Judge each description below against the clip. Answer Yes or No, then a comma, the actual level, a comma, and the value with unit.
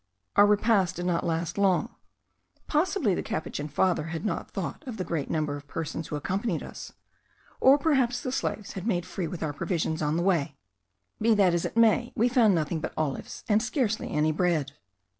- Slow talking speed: No, average, 195 wpm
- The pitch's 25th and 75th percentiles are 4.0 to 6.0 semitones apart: Yes, wide, 5.5 semitones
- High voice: No, medium, 180 Hz